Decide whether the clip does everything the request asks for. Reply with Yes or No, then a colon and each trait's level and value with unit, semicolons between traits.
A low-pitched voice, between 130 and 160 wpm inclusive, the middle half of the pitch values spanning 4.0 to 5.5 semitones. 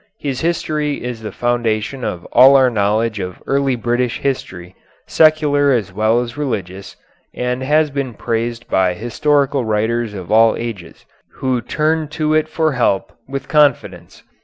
Yes: low, 125 Hz; average, 150 wpm; average, 4.6 semitones